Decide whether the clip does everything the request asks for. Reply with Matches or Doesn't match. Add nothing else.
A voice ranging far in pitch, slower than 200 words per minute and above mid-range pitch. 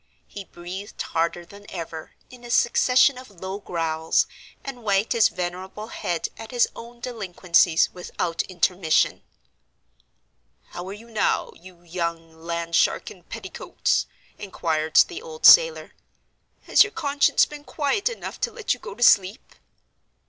Matches